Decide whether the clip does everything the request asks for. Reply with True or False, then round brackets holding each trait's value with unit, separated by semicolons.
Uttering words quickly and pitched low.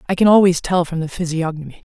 False (220 wpm; 170 Hz)